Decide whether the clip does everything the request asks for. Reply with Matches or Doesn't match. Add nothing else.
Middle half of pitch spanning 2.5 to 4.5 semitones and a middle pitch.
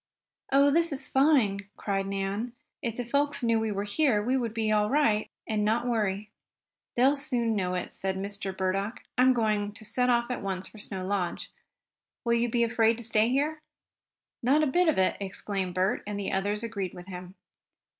Doesn't match